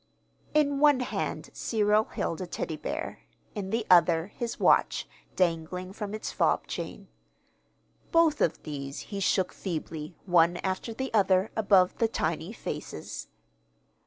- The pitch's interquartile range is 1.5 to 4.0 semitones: No, average, 4.6 semitones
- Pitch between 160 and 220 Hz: Yes, high, 190 Hz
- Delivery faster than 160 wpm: No, slow, 135 wpm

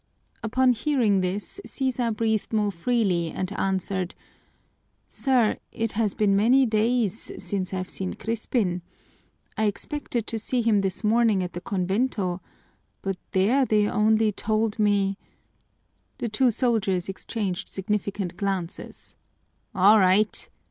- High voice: Yes, high, 210 Hz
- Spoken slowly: Yes, slow, 130 wpm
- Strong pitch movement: No, average, 3.1 semitones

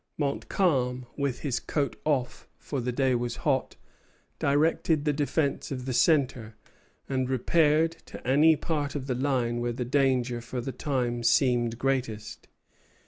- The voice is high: No, low, 130 Hz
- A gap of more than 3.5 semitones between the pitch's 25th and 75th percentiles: No, average, 2.9 semitones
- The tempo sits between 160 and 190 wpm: No, average, 145 wpm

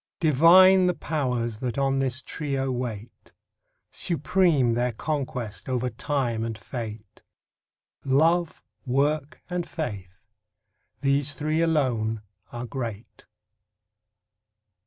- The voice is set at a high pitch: No, low, 130 Hz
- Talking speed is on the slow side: Yes, slow, 95 wpm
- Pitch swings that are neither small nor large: Yes, average, 5.0 semitones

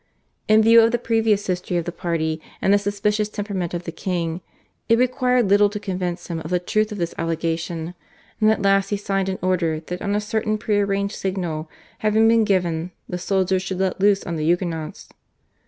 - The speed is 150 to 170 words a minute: No, fast, 205 wpm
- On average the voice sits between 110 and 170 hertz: No, high, 195 Hz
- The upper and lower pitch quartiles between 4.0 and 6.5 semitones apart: No, average, 3.4 semitones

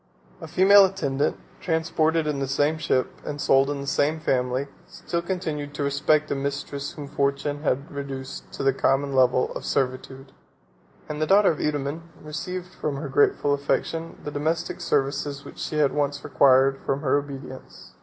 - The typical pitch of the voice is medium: Yes, medium, 145 Hz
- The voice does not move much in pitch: Yes, narrow, 2.2 semitones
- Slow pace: No, average, 170 wpm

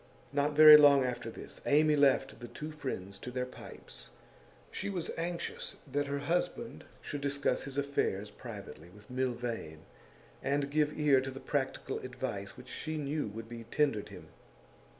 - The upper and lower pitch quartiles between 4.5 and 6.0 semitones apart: No, average, 3.6 semitones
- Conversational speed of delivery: Yes, average, 160 wpm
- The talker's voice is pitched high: No, medium, 140 Hz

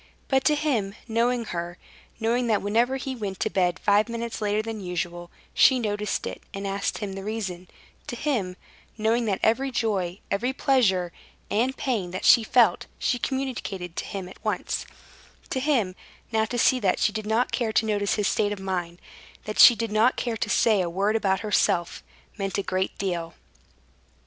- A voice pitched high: Yes, high, 215 Hz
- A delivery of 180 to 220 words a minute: Yes, average, 185 wpm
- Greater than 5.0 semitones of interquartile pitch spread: No, average, 3.6 semitones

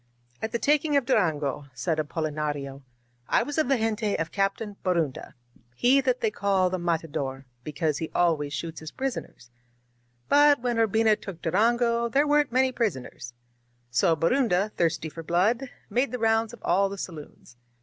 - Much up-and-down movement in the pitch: Yes, wide, 7.2 semitones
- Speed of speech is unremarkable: Yes, average, 165 wpm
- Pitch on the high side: Yes, high, 195 Hz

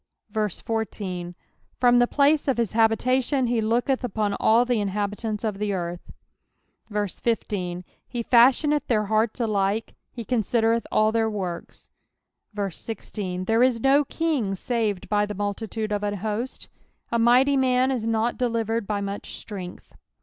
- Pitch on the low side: No, high, 225 Hz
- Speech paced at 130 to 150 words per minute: Yes, average, 145 wpm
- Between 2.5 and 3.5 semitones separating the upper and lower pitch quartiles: Yes, average, 2.9 semitones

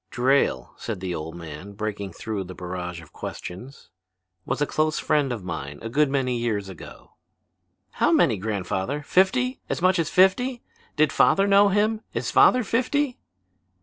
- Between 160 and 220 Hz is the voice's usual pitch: No, low, 125 Hz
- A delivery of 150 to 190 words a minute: Yes, average, 160 wpm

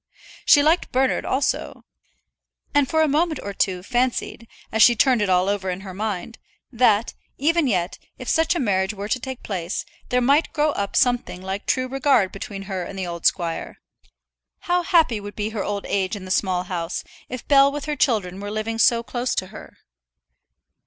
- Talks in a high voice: Yes, high, 220 Hz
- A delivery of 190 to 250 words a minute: Yes, average, 195 wpm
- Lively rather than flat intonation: Yes, wide, 5.8 semitones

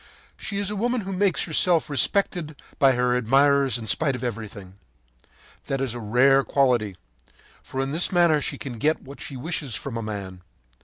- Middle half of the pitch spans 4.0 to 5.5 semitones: Yes, average, 4.9 semitones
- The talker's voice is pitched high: No, low, 135 Hz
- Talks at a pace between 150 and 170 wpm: No, average, 185 wpm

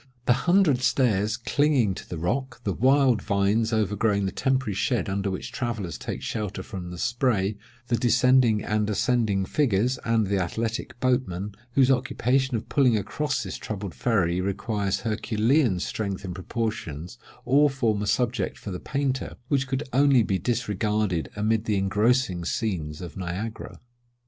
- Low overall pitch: Yes, low, 110 Hz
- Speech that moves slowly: No, average, 155 wpm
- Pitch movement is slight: No, average, 4.3 semitones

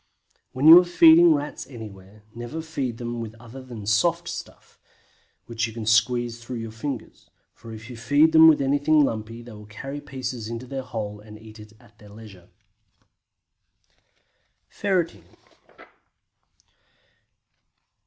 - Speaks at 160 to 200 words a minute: No, average, 140 wpm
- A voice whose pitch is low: Yes, low, 120 Hz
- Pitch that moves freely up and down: No, average, 4.5 semitones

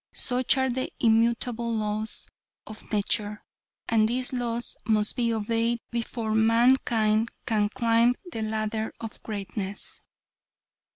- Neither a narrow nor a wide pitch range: No, narrow, 1.6 semitones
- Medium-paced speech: No, slow, 115 wpm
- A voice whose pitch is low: No, high, 225 Hz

